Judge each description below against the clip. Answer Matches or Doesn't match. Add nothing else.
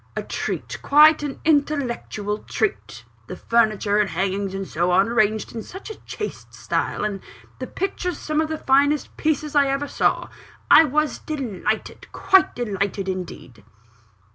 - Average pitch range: Doesn't match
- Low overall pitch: Doesn't match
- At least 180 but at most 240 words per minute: Doesn't match